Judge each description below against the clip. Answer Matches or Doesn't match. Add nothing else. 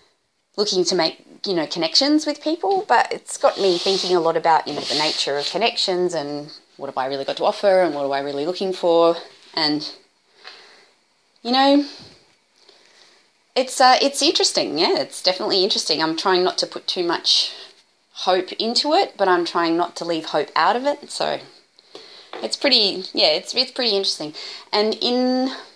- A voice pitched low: Doesn't match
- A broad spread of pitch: Matches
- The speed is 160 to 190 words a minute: Matches